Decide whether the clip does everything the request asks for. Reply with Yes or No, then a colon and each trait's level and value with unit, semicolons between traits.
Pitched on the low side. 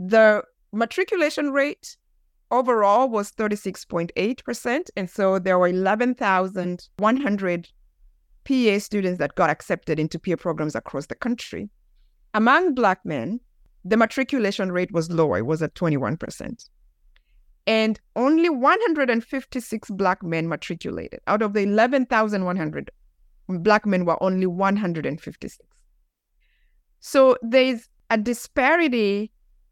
No: high, 210 Hz